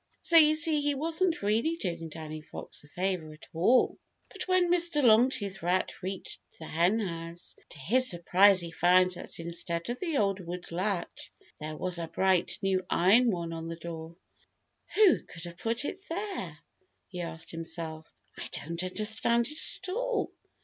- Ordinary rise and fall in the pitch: No, wide, 7.2 semitones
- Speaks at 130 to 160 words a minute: No, average, 170 wpm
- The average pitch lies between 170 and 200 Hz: Yes, medium, 185 Hz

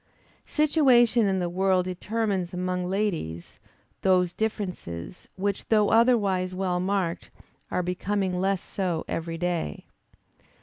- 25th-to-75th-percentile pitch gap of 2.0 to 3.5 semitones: Yes, narrow, 2.5 semitones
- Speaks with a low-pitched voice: No, medium, 185 Hz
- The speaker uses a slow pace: Yes, slow, 115 wpm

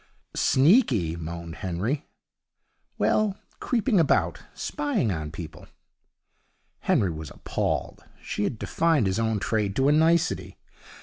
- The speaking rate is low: Yes, slow, 115 wpm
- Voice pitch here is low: Yes, low, 110 Hz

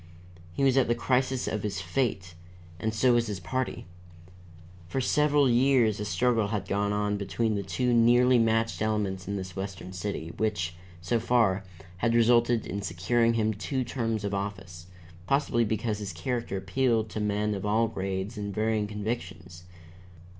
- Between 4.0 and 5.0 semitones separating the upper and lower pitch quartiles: No, average, 3.3 semitones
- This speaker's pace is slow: No, average, 165 wpm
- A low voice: Yes, low, 110 Hz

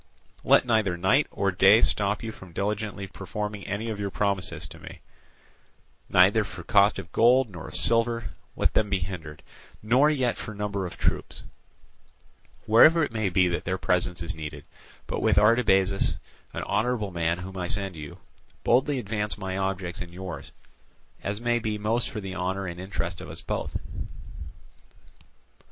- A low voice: Yes, low, 100 Hz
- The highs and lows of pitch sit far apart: No, average, 3.2 semitones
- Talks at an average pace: Yes, average, 165 wpm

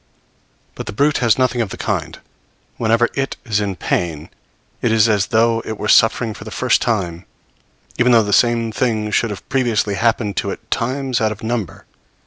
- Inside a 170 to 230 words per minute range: Yes, average, 190 wpm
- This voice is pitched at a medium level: No, low, 115 Hz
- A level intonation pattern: Yes, narrow, 2.3 semitones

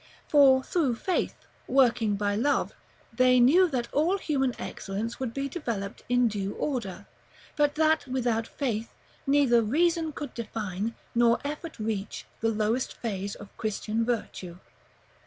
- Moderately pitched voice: No, high, 240 Hz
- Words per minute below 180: Yes, average, 140 wpm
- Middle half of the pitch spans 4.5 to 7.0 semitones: Yes, average, 4.8 semitones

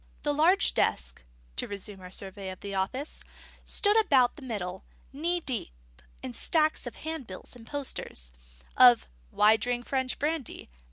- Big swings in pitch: Yes, wide, 7.3 semitones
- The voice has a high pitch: Yes, high, 245 Hz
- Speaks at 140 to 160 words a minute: Yes, average, 150 wpm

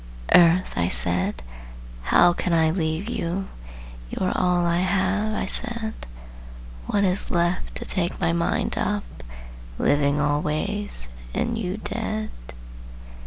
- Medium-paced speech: No, slow, 125 wpm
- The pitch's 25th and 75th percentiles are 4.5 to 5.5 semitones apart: No, average, 4.1 semitones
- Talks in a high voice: No, medium, 180 Hz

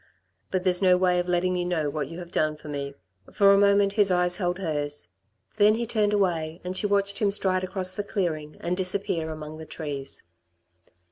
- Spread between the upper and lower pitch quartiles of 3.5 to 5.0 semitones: Yes, average, 4.0 semitones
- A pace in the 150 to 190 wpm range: No, fast, 205 wpm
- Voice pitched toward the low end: No, medium, 180 Hz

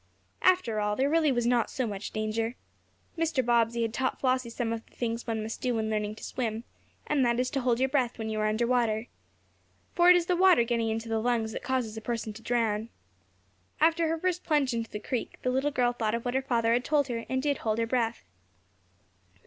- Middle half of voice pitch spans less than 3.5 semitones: Yes, average, 2.7 semitones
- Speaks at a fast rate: Yes, fast, 230 wpm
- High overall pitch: Yes, high, 235 Hz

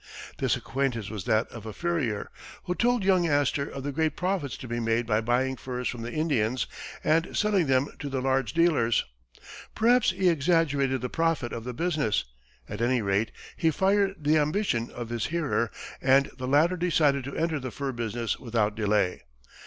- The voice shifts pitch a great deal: Yes, wide, 5.7 semitones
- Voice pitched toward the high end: No, low, 135 Hz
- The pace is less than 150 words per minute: No, average, 185 wpm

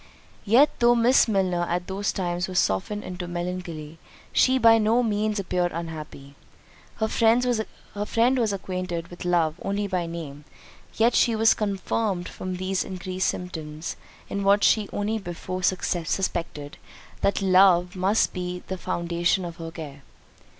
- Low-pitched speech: No, medium, 185 Hz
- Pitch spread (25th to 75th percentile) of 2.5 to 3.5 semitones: Yes, average, 3.2 semitones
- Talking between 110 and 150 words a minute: Yes, average, 145 wpm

